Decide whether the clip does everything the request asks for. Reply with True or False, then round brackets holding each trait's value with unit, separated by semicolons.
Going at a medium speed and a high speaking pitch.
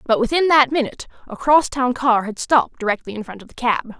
False (225 wpm; 245 Hz)